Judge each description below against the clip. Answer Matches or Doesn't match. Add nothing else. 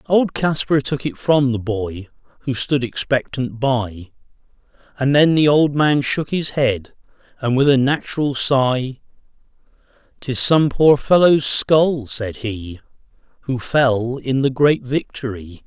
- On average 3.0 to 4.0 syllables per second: Matches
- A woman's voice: Doesn't match